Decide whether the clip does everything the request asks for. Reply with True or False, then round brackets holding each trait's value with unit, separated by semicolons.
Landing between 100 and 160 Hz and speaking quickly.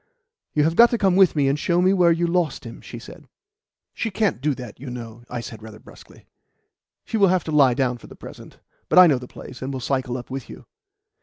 True (140 Hz; 245 wpm)